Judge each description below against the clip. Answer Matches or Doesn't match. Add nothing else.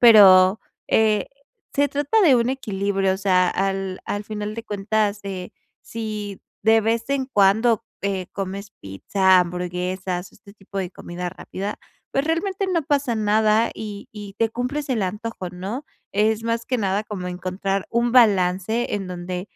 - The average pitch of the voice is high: Matches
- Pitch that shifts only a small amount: Doesn't match